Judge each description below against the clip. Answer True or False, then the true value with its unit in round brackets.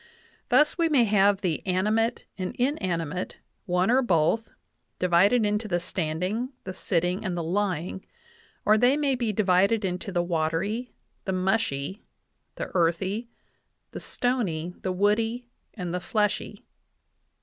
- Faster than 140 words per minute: False (135 wpm)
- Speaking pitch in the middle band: False (195 Hz)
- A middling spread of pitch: True (4.1 semitones)